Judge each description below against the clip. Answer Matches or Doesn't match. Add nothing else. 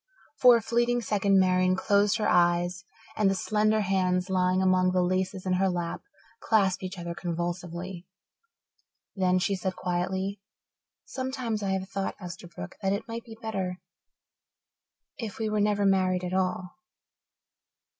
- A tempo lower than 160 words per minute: Matches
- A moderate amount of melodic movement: Doesn't match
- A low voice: Doesn't match